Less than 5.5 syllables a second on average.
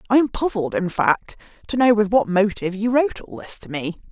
No: 5.9 syllables/s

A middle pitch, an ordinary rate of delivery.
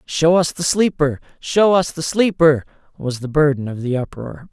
Yes: medium, 150 Hz; average, 185 wpm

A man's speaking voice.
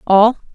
No: female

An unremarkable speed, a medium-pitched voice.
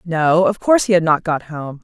No: fast, 260 wpm; medium, 170 Hz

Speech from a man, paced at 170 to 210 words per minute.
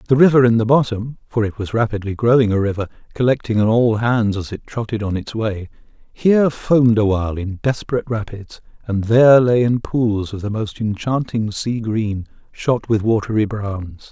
Yes: male; average, 185 wpm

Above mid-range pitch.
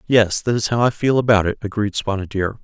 No: low, 110 Hz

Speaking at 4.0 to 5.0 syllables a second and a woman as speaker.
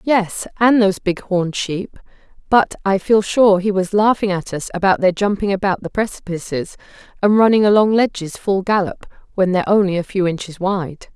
No: 5.2 syllables/s; female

